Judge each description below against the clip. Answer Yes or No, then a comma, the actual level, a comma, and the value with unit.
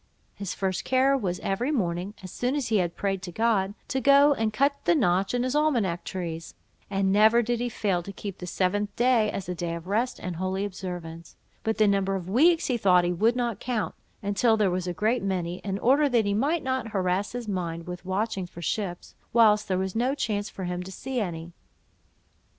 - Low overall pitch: No, high, 200 Hz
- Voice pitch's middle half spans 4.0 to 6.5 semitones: Yes, average, 4.6 semitones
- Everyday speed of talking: No, fast, 220 wpm